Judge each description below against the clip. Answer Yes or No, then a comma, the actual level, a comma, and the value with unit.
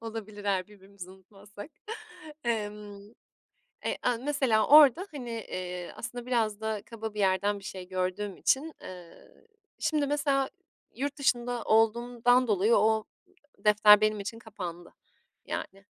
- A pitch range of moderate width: Yes, average, 3.5 semitones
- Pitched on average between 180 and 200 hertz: No, high, 215 Hz